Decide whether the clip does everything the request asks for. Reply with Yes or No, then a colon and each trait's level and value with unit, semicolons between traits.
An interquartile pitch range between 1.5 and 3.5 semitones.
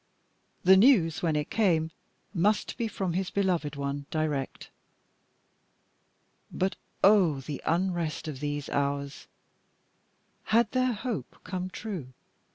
No: average, 5.3 semitones